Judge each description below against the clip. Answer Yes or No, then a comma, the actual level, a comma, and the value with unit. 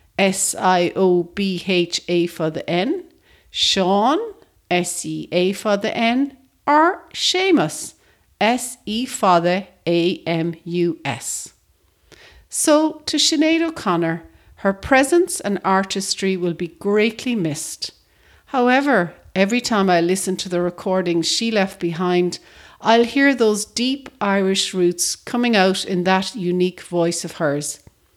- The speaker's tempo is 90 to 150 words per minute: Yes, slow, 135 wpm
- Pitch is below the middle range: No, high, 190 Hz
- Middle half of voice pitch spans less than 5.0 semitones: No, wide, 5.6 semitones